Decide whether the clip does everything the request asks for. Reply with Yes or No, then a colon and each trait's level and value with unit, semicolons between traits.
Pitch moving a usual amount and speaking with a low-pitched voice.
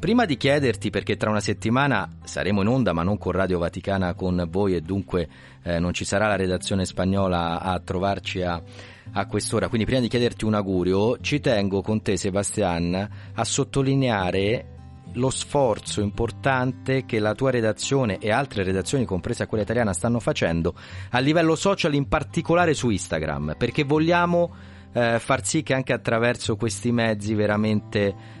Yes: average, 4.5 semitones; low, 105 Hz